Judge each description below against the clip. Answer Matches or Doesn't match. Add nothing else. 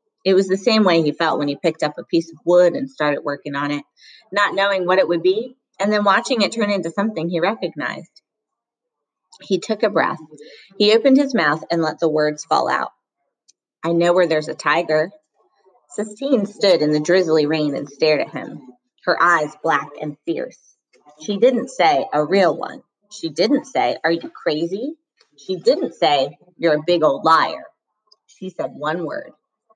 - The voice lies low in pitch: Doesn't match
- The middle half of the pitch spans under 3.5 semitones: Doesn't match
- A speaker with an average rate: Matches